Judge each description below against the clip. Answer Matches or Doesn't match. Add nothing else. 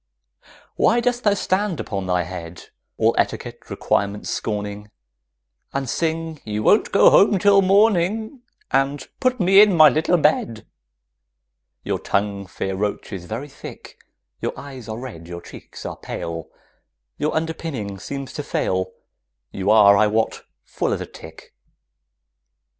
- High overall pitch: Doesn't match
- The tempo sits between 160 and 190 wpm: Doesn't match